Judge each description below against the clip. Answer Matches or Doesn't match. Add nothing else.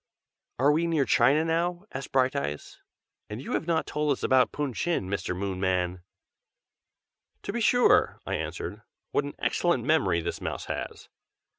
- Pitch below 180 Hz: Matches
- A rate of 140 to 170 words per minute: Matches